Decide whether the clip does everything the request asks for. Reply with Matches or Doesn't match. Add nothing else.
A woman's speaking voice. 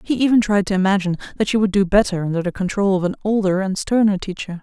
Matches